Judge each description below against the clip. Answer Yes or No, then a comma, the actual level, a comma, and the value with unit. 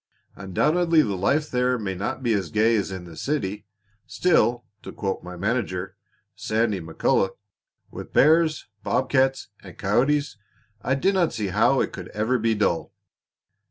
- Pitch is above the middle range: No, low, 115 Hz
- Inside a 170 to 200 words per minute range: No, average, 155 wpm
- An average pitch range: No, wide, 5.9 semitones